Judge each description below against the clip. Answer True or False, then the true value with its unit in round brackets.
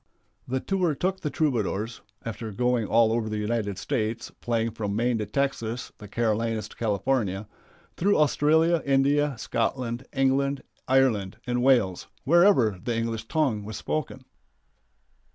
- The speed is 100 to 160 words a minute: True (135 wpm)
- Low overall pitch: True (120 Hz)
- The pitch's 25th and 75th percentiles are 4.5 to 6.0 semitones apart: False (4.0 semitones)